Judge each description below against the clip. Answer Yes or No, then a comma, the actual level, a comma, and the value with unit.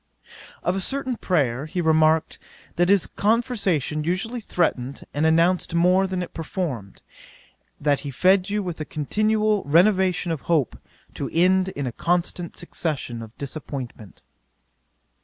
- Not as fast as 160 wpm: Yes, average, 140 wpm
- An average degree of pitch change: Yes, average, 4.2 semitones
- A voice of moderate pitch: Yes, medium, 170 Hz